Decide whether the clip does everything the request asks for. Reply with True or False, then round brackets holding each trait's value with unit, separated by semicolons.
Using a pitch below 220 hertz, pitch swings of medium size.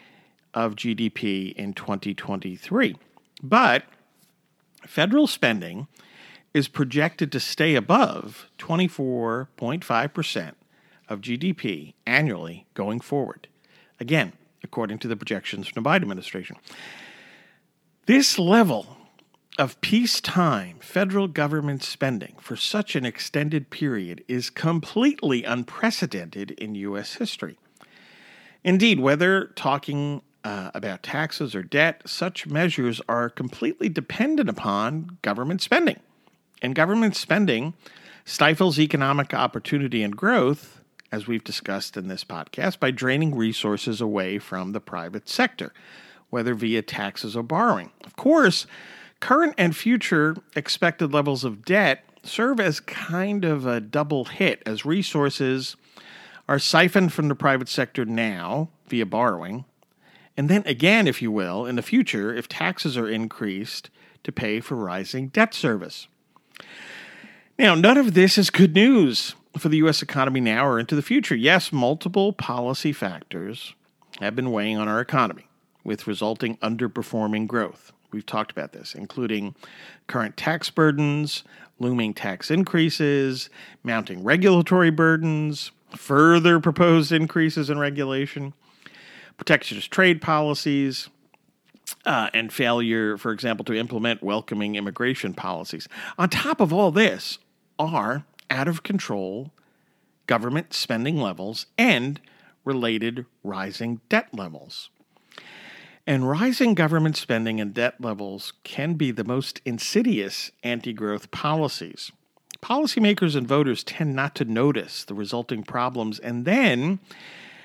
False (140 Hz; 6.7 semitones)